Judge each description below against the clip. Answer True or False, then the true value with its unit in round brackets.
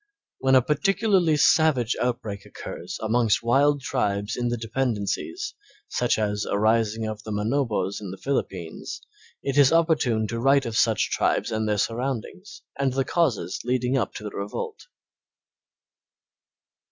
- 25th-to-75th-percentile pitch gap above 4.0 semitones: True (4.4 semitones)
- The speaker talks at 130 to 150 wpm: True (145 wpm)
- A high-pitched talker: False (120 Hz)